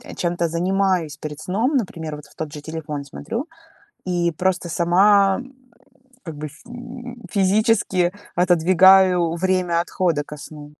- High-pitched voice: No, medium, 175 Hz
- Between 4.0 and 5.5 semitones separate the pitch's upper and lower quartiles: No, average, 3.4 semitones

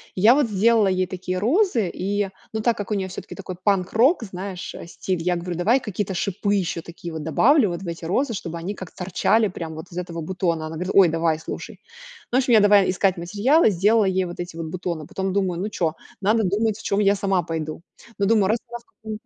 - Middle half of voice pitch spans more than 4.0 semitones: No, average, 3.5 semitones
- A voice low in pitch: No, high, 190 Hz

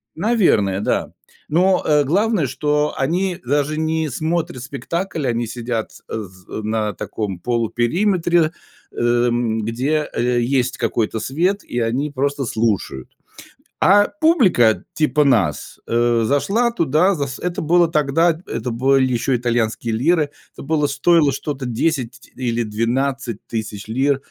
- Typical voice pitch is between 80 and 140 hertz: Yes, low, 135 Hz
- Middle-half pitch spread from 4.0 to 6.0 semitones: Yes, wide, 5.4 semitones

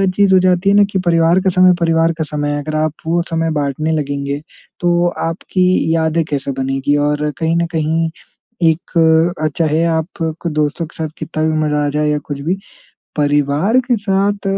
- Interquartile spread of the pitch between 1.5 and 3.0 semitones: Yes, narrow, 2.6 semitones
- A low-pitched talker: No, medium, 160 Hz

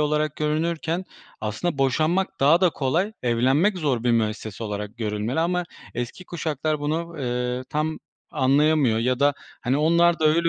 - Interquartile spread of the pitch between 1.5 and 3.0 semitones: No, average, 5.0 semitones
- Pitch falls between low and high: Yes, medium, 150 Hz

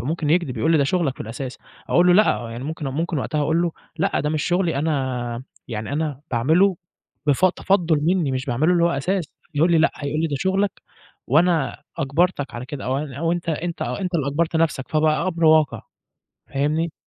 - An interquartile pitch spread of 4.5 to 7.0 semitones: No, average, 3.8 semitones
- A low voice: No, medium, 155 Hz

